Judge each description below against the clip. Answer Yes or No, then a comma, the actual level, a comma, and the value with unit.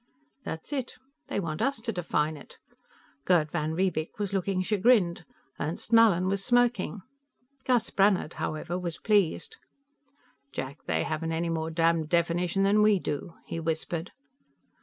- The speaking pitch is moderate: Yes, medium, 180 Hz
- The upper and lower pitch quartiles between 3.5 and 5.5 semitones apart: Yes, average, 4.1 semitones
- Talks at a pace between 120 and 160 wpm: Yes, average, 140 wpm